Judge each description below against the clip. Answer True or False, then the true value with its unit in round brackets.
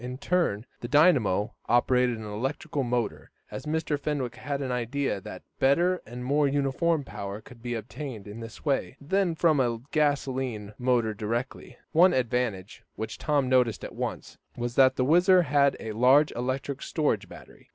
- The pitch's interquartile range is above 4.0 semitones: False (3.7 semitones)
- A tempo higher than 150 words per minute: True (165 wpm)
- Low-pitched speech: True (130 Hz)